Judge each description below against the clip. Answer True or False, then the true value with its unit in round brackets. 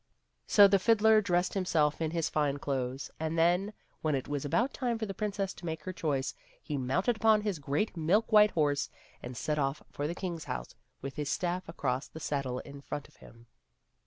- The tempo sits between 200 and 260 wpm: True (205 wpm)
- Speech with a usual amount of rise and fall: False (5.7 semitones)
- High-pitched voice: False (160 Hz)